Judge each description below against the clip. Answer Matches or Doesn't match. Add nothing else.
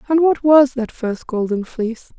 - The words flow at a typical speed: Matches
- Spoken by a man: Doesn't match